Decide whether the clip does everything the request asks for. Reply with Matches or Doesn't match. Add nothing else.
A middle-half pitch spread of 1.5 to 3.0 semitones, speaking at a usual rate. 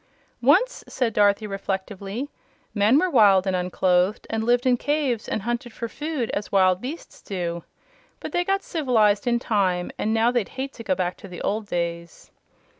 Doesn't match